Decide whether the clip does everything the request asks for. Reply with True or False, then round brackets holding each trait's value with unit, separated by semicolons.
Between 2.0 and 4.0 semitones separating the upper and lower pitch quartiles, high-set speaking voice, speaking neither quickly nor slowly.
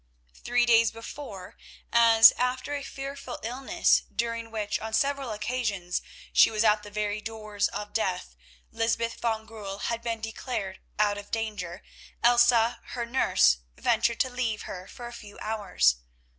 True (2.4 semitones; 225 Hz; 150 wpm)